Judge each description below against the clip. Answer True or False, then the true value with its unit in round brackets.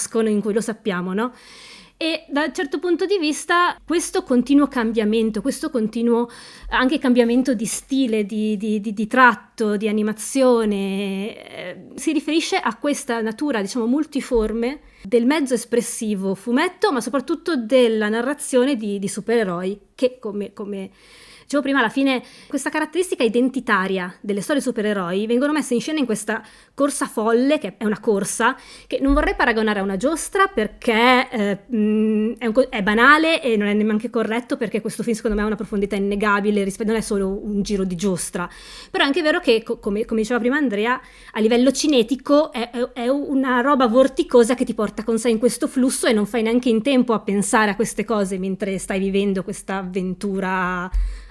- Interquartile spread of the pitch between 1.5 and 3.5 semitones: False (4.0 semitones)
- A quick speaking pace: True (175 wpm)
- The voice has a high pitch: True (235 Hz)